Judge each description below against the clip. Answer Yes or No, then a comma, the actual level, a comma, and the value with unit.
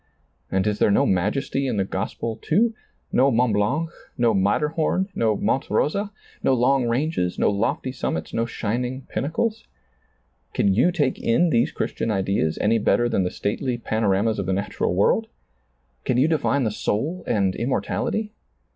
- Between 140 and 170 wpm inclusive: Yes, average, 165 wpm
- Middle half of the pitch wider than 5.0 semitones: Yes, wide, 5.6 semitones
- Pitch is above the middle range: No, low, 115 Hz